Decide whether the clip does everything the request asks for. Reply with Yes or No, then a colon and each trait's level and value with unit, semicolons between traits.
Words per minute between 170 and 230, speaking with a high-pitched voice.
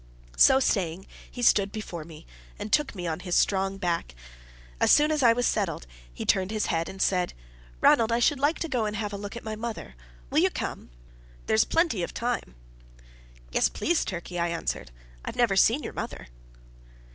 Yes: average, 195 wpm; high, 205 Hz